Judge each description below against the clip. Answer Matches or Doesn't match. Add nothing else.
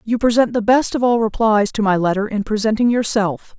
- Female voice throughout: Matches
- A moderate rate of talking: Doesn't match